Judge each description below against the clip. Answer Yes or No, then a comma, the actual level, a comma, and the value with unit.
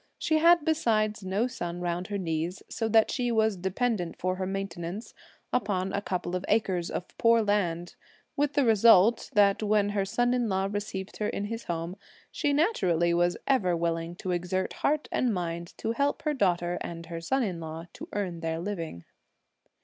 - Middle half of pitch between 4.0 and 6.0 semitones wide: Yes, average, 4.4 semitones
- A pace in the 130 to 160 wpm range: No, average, 185 wpm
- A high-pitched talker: Yes, high, 195 Hz